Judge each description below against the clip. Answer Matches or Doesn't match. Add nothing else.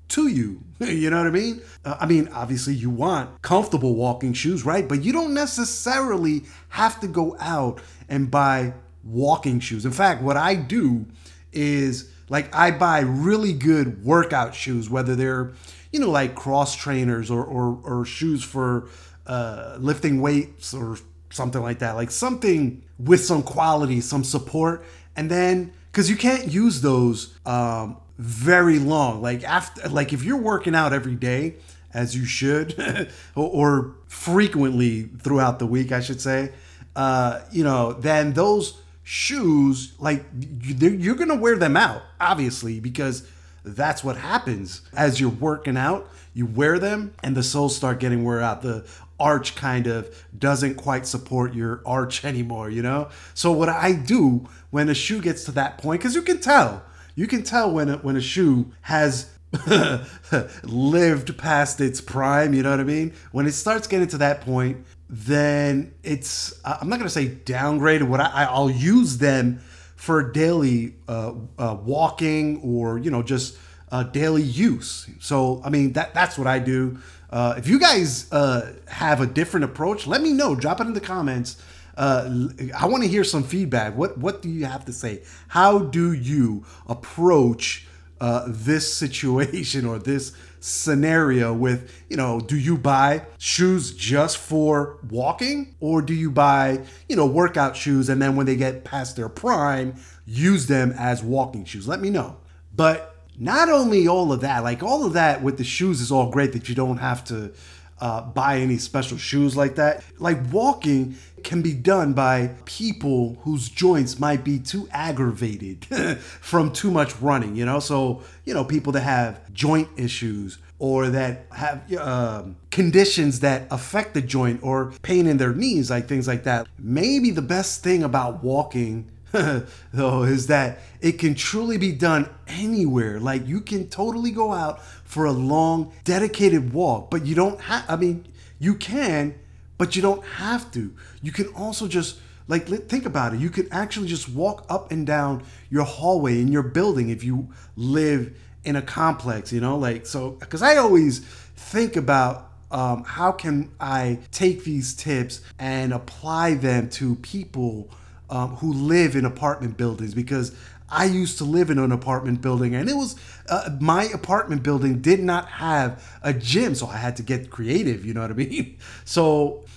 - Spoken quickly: Doesn't match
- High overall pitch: Doesn't match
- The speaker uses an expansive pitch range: Doesn't match